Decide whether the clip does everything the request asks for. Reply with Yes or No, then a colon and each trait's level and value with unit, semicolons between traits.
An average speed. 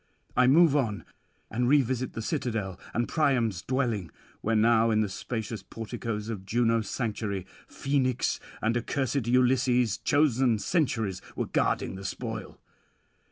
No: slow, 130 wpm